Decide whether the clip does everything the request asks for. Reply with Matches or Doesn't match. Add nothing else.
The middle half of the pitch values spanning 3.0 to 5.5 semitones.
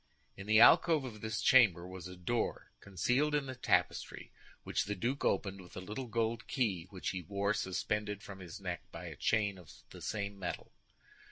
Matches